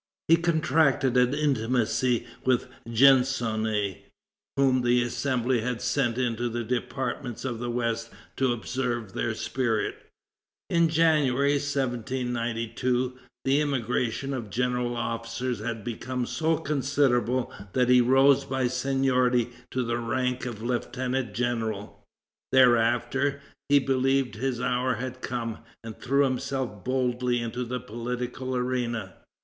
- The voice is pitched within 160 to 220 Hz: No, low, 125 Hz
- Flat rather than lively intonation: Yes, narrow, 2.0 semitones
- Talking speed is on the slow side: Yes, slow, 120 wpm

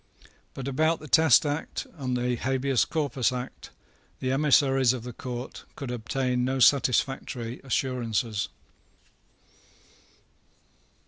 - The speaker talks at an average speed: No, slow, 110 wpm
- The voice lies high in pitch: No, low, 130 Hz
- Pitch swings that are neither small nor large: No, narrow, 1.8 semitones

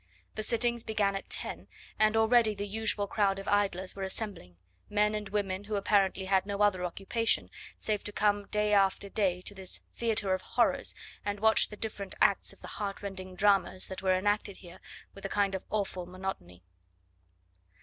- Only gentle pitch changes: Yes, narrow, 1.7 semitones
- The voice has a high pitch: Yes, high, 200 Hz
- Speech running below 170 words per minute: No, average, 180 wpm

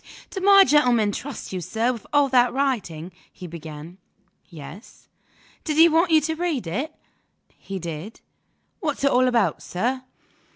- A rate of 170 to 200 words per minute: No, average, 155 wpm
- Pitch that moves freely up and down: Yes, wide, 8.4 semitones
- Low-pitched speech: No, high, 245 Hz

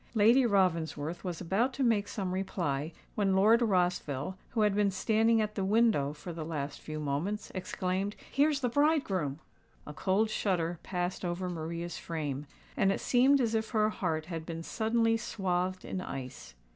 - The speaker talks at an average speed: Yes, average, 170 wpm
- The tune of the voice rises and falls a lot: No, average, 4.9 semitones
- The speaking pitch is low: No, high, 190 Hz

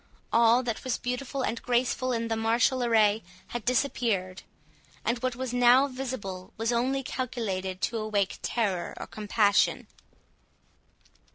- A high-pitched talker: Yes, high, 235 Hz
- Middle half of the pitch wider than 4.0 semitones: No, average, 2.9 semitones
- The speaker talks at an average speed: No, slow, 130 wpm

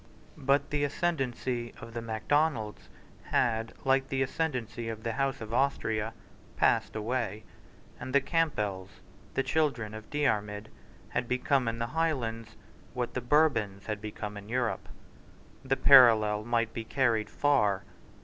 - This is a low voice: Yes, low, 120 Hz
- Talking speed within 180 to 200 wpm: No, average, 140 wpm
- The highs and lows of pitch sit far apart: No, average, 3.8 semitones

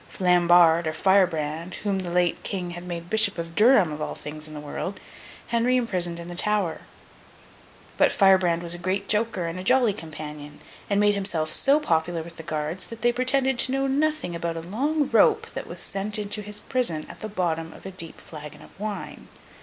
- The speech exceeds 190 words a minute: Yes, average, 200 wpm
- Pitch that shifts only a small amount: No, average, 4.2 semitones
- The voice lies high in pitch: No, medium, 180 Hz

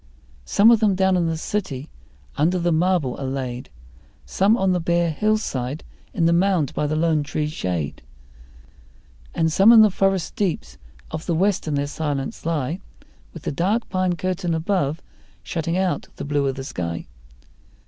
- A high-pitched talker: No, medium, 165 Hz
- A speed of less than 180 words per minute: Yes, average, 170 wpm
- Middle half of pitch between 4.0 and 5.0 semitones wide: Yes, average, 4.5 semitones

